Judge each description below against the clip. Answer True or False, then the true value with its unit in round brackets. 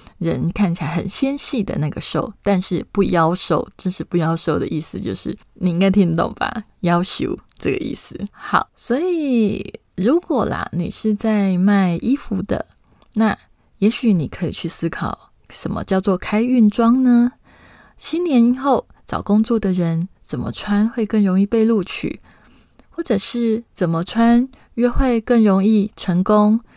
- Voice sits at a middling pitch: False (210 Hz)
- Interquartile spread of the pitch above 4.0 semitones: True (4.4 semitones)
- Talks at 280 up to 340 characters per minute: False (225 characters per minute)